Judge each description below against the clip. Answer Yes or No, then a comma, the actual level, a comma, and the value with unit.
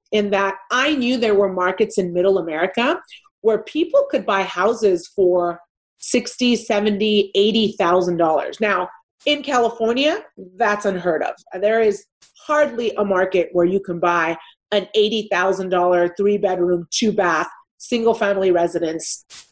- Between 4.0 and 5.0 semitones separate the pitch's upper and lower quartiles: Yes, average, 4.4 semitones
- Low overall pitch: No, high, 205 Hz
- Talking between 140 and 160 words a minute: Yes, average, 145 wpm